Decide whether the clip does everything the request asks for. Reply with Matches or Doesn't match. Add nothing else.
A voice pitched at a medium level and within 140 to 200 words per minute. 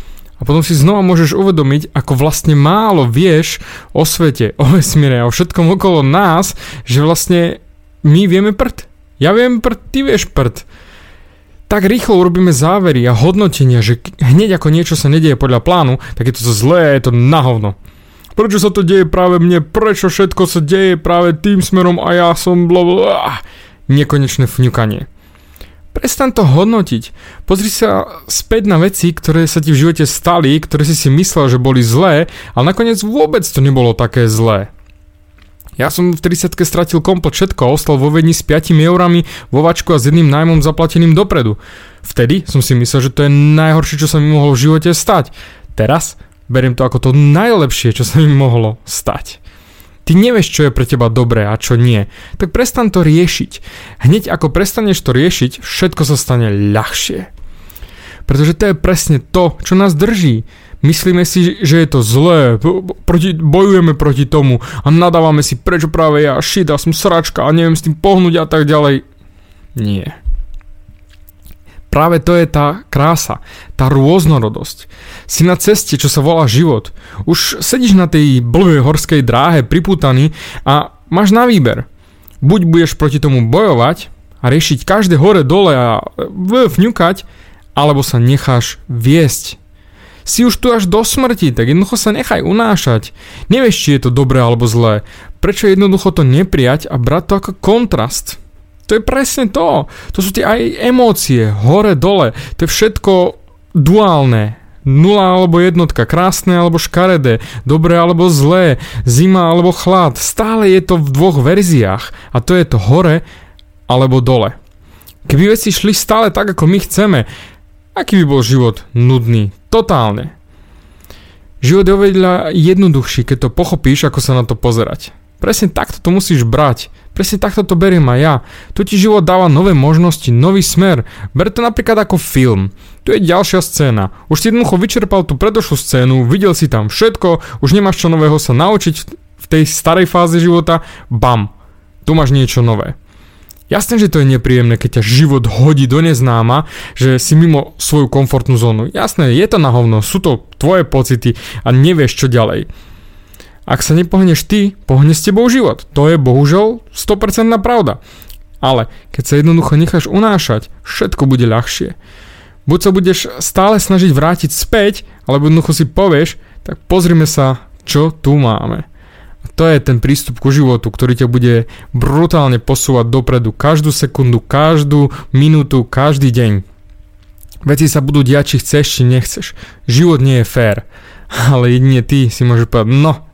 Matches